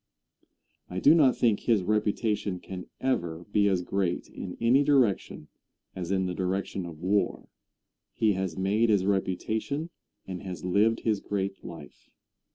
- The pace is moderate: Yes, average, 150 wpm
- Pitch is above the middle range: No, low, 100 Hz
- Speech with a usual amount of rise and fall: Yes, average, 3.3 semitones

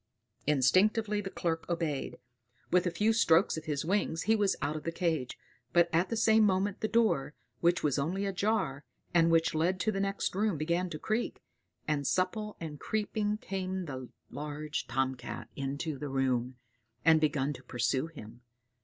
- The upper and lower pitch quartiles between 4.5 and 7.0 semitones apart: Yes, average, 5.2 semitones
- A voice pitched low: No, medium, 165 Hz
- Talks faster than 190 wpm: No, average, 170 wpm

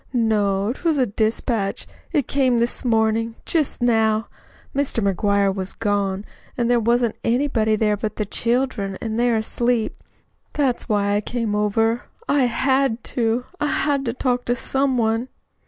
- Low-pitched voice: No, high, 230 Hz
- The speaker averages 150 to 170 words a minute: Yes, average, 155 wpm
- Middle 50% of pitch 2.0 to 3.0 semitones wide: Yes, average, 2.7 semitones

